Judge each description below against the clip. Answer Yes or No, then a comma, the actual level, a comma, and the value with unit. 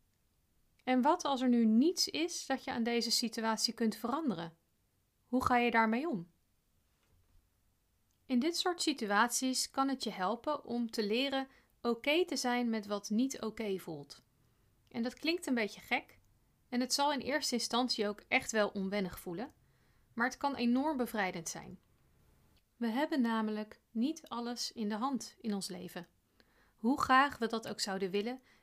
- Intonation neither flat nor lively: Yes, average, 4.6 semitones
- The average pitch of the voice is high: Yes, high, 235 Hz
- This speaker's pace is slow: No, average, 170 wpm